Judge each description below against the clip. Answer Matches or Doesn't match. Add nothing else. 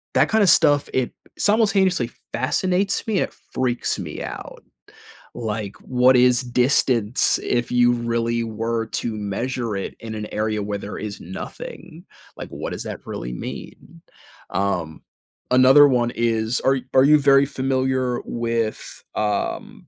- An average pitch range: Matches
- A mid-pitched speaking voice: Doesn't match